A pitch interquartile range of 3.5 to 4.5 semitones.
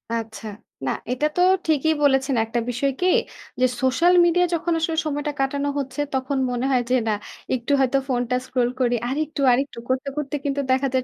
No: average, 2.8 semitones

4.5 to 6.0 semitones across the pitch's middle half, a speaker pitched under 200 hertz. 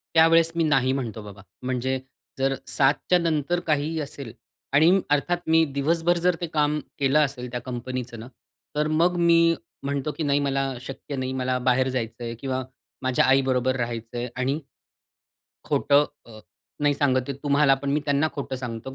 No: average, 2.9 semitones; low, 135 Hz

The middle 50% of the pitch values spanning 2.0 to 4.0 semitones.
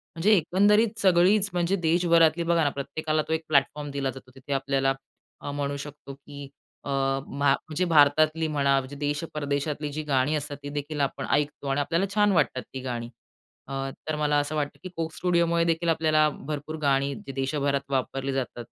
Yes: average, 2.7 semitones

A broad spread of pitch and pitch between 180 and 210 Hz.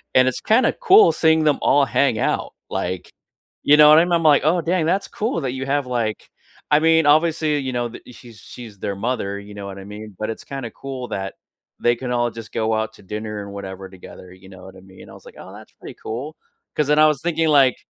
No: wide, 6.7 semitones; low, 125 Hz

